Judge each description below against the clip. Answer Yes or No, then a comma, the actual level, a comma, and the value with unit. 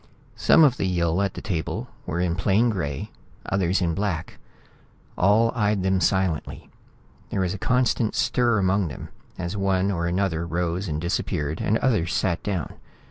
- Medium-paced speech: Yes, average, 165 wpm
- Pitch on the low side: Yes, very low, 95 Hz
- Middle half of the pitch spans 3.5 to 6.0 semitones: No, average, 3.0 semitones